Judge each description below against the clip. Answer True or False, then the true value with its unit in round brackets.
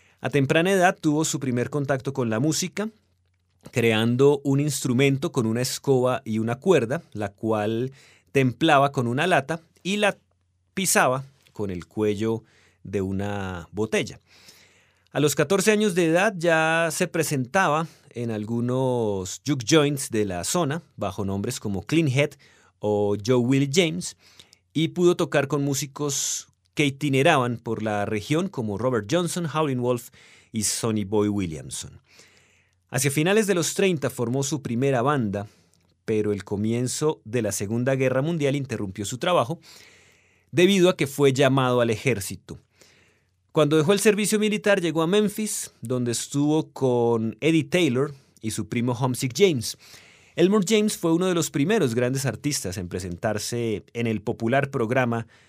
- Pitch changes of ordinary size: False (6.5 semitones)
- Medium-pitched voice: False (130 Hz)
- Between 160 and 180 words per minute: False (150 wpm)